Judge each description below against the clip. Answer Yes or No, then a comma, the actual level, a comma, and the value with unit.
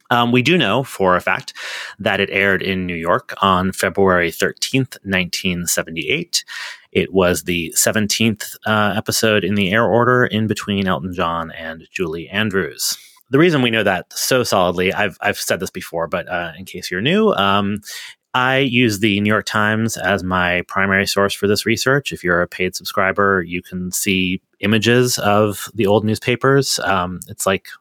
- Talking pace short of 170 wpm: No, average, 175 wpm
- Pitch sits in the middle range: No, low, 100 Hz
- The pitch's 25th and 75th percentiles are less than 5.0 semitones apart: Yes, average, 3.4 semitones